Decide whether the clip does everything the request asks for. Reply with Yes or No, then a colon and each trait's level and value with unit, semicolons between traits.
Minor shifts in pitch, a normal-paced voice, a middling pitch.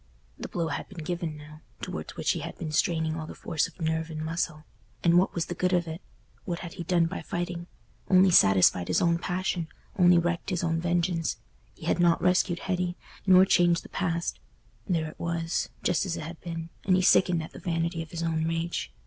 No: narrow, 1.5 semitones; fast, 210 wpm; medium, 170 Hz